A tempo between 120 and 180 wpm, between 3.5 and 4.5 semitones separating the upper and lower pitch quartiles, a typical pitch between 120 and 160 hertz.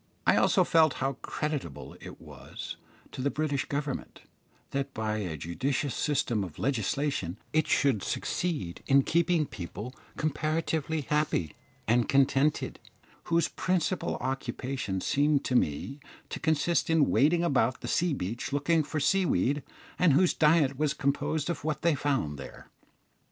Yes: average, 145 wpm; average, 3.8 semitones; medium, 140 Hz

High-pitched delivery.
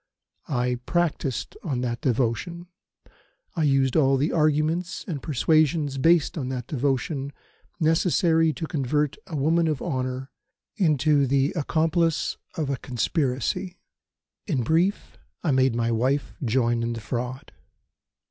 No: medium, 140 Hz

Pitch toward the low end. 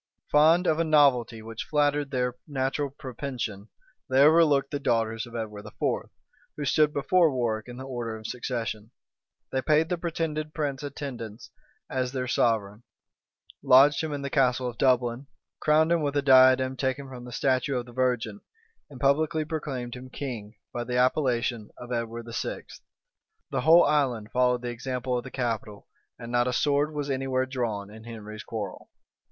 Yes: low, 130 Hz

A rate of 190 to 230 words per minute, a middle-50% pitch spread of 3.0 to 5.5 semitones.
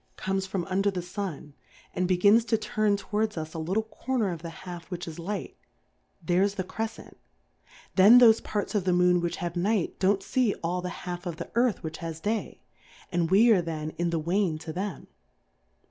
Yes: average, 200 wpm; average, 3.3 semitones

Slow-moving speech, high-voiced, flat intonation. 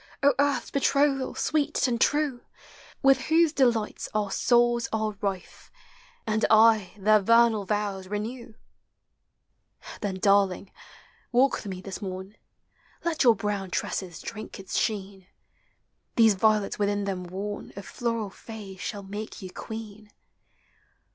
No: slow, 130 wpm; high, 215 Hz; average, 3.2 semitones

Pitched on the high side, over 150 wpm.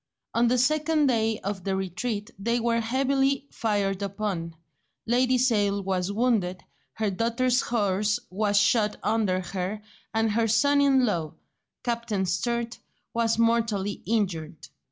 No: high, 220 Hz; slow, 135 wpm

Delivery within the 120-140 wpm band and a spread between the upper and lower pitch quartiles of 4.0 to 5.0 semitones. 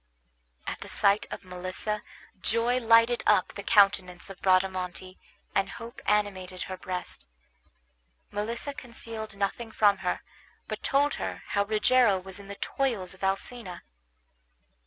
No: slow, 135 wpm; average, 3.5 semitones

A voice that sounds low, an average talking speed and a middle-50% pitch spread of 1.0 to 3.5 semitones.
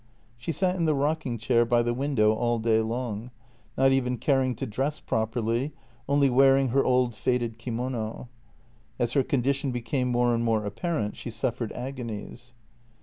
Yes: low, 125 Hz; average, 160 wpm; narrow, 2.6 semitones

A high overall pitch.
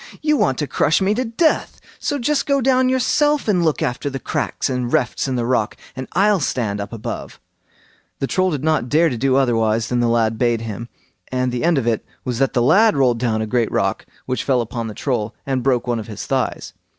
No: low, 130 Hz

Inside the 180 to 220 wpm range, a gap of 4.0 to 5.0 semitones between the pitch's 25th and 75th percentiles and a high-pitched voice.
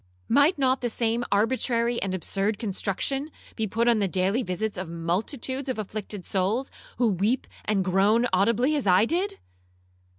No: average, 160 wpm; average, 4.5 semitones; high, 220 Hz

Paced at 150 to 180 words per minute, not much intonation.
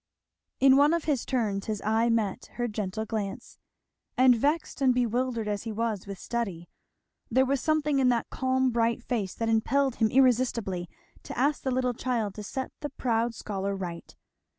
No: average, 175 wpm; average, 3.5 semitones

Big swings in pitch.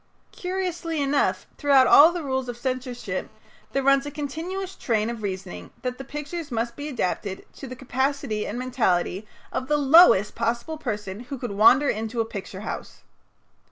No: average, 4.6 semitones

